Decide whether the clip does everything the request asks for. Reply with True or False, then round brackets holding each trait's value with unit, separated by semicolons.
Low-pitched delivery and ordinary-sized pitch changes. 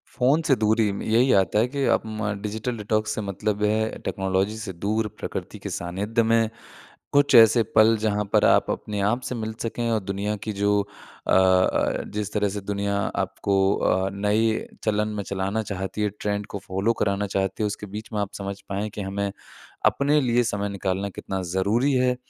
False (105 Hz; 2.0 semitones)